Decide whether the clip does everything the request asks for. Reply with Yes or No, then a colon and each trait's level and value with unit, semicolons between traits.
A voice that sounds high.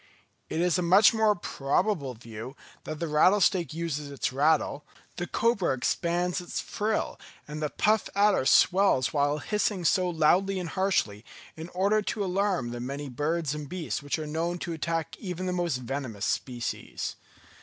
No: medium, 170 Hz